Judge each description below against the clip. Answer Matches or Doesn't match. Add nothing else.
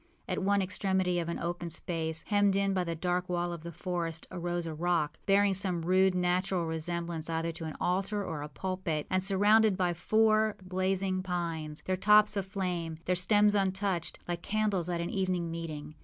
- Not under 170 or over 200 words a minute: Matches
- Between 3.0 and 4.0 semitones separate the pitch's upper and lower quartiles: Doesn't match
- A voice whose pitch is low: Doesn't match